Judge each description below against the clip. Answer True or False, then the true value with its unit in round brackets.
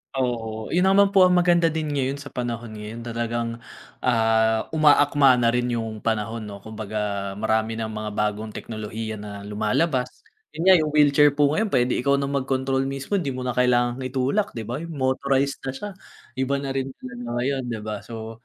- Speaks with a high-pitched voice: False (125 Hz)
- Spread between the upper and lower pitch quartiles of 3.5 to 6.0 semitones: True (4.0 semitones)